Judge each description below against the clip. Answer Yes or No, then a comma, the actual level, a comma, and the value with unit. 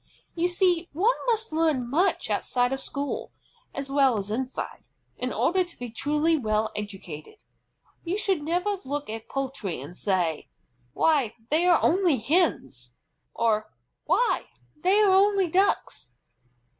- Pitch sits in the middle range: No, very high, 290 Hz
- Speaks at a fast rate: No, average, 140 wpm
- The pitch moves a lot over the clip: Yes, wide, 8.0 semitones